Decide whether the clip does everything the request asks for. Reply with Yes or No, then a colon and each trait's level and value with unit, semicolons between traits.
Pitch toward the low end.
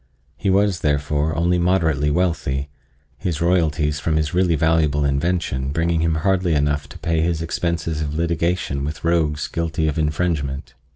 Yes: very low, 80 Hz